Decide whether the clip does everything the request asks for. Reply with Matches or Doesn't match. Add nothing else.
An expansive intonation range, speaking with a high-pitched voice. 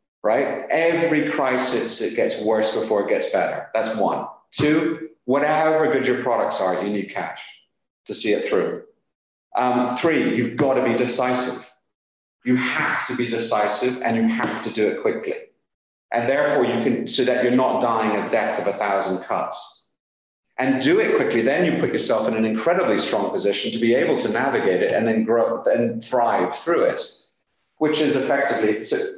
Doesn't match